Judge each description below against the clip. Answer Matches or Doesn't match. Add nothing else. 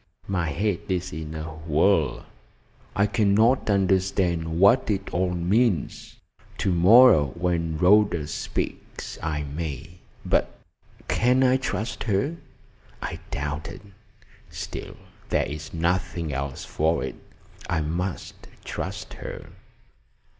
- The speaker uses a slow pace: Matches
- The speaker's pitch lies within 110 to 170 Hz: Doesn't match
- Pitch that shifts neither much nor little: Matches